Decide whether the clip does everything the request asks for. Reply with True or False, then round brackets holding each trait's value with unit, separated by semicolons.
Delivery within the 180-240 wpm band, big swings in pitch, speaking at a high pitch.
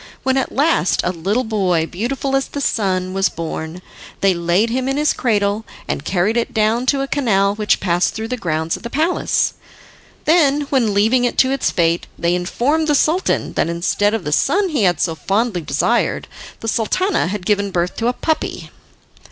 True (190 wpm; 6.6 semitones; 215 Hz)